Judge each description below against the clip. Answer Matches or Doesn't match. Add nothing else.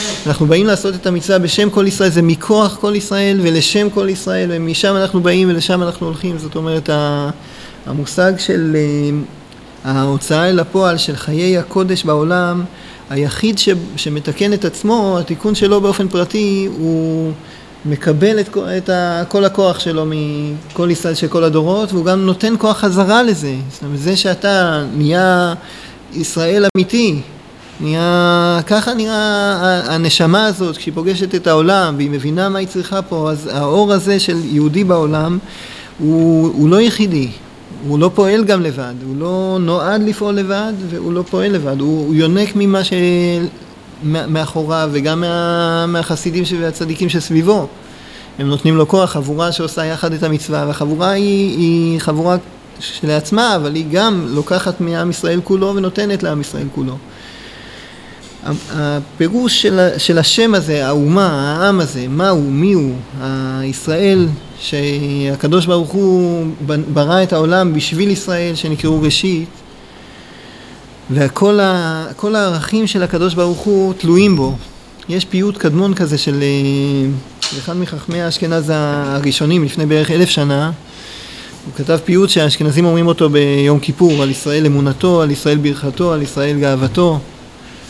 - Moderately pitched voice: Matches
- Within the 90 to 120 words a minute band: Doesn't match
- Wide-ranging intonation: Doesn't match